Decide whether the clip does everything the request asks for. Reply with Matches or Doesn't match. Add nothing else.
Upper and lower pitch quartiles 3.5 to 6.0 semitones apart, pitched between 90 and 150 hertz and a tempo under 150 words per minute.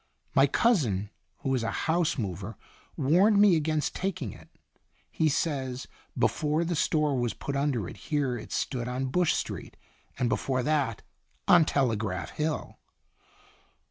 Matches